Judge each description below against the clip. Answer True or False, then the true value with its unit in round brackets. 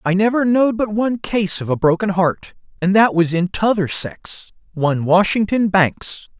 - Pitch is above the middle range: True (195 Hz)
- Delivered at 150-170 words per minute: False (180 wpm)